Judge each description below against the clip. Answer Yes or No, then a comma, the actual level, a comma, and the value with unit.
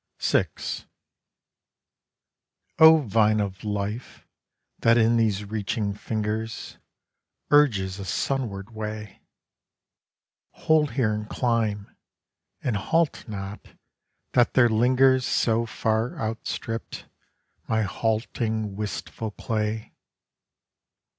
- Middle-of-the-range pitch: No, low, 110 Hz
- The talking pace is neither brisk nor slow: No, slow, 90 wpm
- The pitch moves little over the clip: Yes, narrow, 2.0 semitones